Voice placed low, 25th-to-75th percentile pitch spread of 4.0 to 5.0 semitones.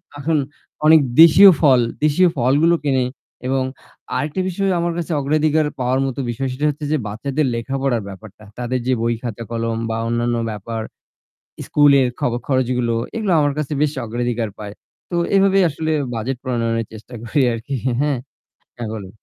Yes: low, 130 Hz; average, 4.5 semitones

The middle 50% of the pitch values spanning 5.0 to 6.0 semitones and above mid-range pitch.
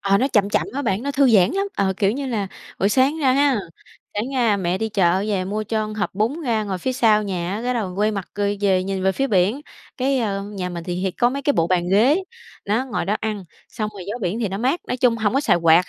No: average, 4.6 semitones; high, 210 Hz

